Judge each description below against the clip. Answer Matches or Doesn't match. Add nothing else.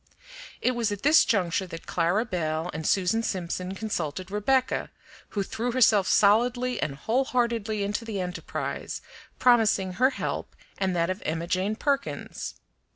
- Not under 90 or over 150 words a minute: Matches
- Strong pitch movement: Doesn't match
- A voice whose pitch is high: Matches